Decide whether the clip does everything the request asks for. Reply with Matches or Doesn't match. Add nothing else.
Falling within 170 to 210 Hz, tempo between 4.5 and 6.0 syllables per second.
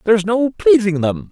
Matches